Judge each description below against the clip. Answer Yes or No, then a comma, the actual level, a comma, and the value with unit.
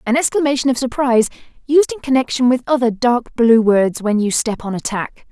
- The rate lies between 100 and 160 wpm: No, fast, 205 wpm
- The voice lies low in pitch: No, high, 245 Hz